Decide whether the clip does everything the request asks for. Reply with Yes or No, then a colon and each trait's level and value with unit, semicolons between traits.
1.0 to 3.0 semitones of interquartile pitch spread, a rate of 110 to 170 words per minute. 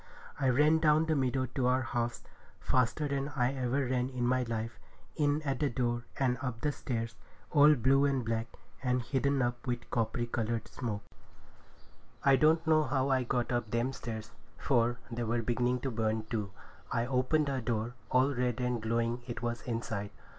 No: narrow, 2.5 semitones; average, 180 wpm